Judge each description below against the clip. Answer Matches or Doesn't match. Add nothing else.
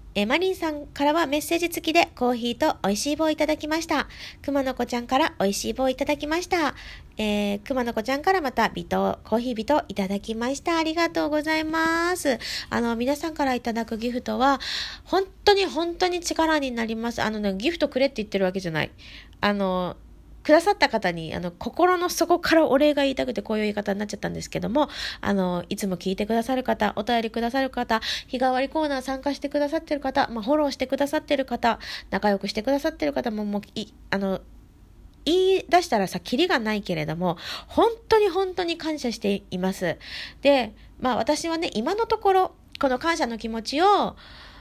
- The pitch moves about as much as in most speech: Doesn't match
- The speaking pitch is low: Doesn't match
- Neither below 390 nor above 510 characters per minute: Matches